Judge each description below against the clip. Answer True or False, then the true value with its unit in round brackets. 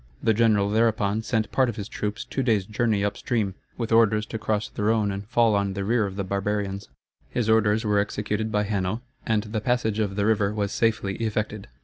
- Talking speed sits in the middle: False (215 wpm)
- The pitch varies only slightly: True (1.7 semitones)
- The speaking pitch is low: True (105 Hz)